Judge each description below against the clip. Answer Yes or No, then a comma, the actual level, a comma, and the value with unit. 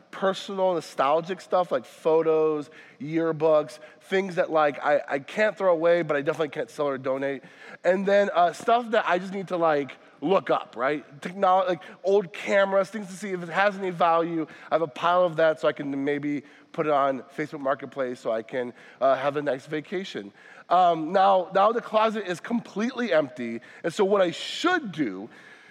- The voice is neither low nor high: Yes, medium, 170 Hz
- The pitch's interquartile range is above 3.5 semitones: Yes, average, 4.4 semitones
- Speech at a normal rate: Yes, average, 195 wpm